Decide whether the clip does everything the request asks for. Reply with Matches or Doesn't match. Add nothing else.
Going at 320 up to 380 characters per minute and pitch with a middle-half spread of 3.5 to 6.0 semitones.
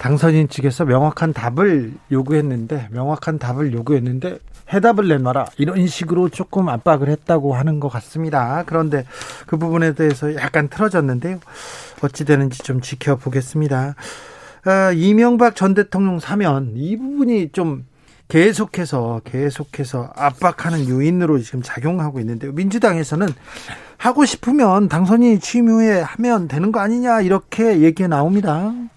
Matches